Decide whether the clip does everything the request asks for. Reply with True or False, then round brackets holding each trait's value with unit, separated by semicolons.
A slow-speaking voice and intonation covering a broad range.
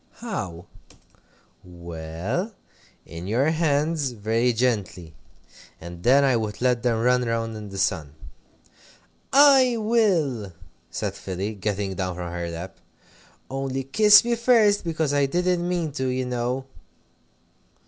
True (130 wpm; 8.9 semitones)